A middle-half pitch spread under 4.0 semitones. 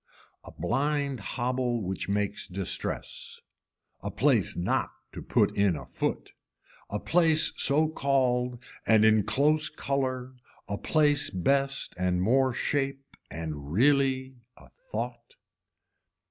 No: average, 5.3 semitones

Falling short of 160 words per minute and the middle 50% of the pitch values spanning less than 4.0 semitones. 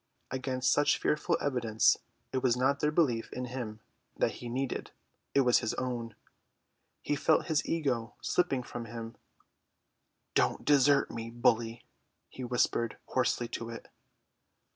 Yes: average, 140 wpm; average, 2.8 semitones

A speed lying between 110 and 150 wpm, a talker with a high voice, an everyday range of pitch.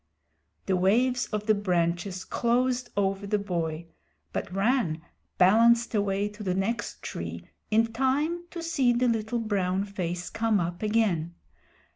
Yes: average, 140 wpm; high, 205 Hz; average, 4.3 semitones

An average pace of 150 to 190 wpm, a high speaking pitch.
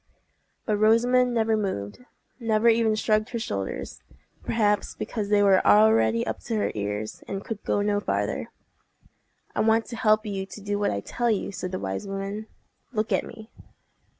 Yes: average, 165 wpm; high, 210 Hz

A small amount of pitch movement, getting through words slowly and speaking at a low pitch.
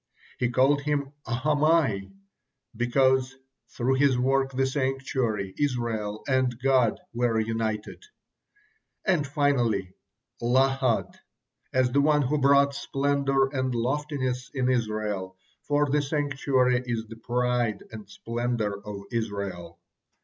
No: average, 3.3 semitones; slow, 115 wpm; low, 125 Hz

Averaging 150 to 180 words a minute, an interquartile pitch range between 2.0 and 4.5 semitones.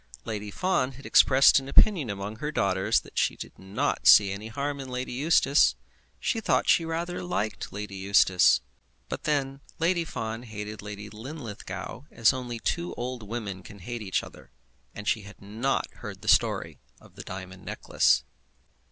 No: average, 170 wpm; average, 5.2 semitones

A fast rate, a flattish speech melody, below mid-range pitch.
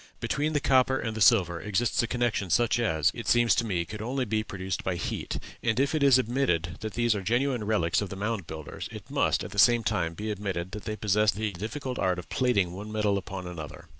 No: fast, 235 wpm; average, 4.4 semitones; low, 105 Hz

